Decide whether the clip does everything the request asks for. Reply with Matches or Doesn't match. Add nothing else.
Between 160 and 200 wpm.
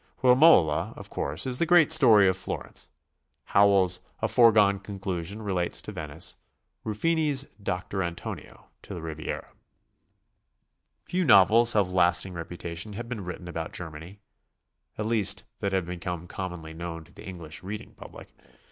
Doesn't match